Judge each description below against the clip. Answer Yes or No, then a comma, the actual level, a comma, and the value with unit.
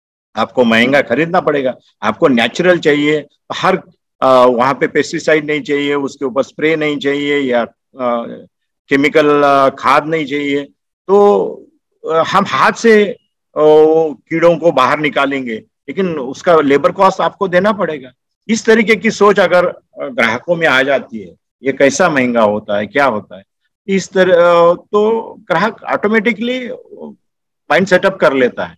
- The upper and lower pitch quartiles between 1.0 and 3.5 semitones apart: No, wide, 5.5 semitones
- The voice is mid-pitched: Yes, medium, 160 Hz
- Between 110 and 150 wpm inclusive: Yes, average, 140 wpm